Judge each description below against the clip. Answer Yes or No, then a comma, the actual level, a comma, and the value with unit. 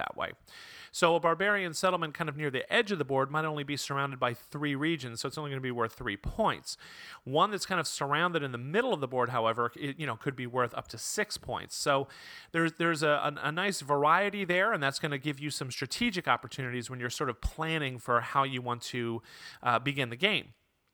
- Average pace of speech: No, fast, 240 wpm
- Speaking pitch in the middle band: Yes, medium, 145 Hz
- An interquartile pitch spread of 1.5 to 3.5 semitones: No, average, 4.6 semitones